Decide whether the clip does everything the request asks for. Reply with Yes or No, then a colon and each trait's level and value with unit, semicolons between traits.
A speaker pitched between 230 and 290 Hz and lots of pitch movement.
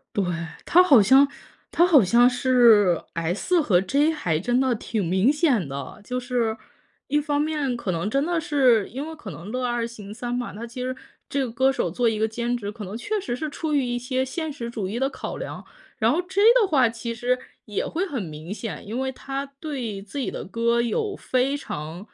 No: high, 245 Hz; average, 4.6 semitones